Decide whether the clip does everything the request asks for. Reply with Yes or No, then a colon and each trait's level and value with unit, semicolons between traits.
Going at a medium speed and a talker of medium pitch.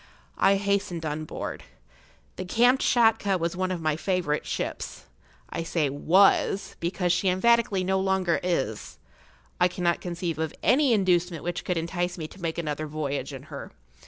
Yes: average, 160 wpm; medium, 175 Hz